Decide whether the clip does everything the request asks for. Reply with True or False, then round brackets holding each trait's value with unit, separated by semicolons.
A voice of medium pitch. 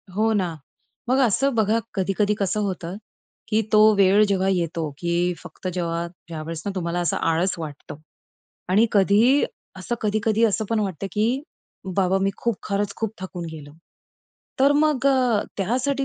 False (200 Hz)